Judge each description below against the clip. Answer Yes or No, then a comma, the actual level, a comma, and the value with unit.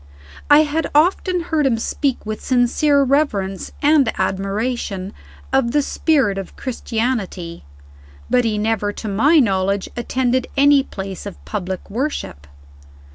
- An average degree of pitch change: No, wide, 6.2 semitones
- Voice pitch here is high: Yes, high, 240 Hz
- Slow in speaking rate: Yes, slow, 130 wpm